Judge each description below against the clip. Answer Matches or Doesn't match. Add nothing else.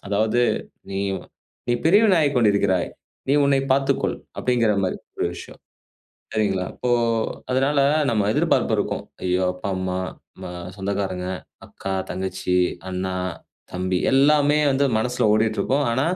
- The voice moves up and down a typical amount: Doesn't match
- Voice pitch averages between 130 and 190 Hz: Doesn't match